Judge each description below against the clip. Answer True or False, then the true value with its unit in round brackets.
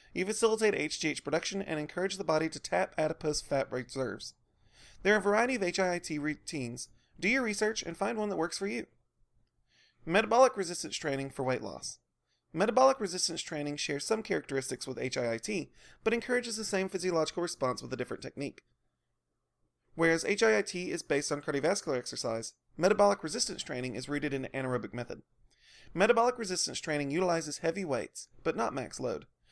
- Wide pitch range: True (6.2 semitones)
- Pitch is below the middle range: False (165 Hz)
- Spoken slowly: False (165 wpm)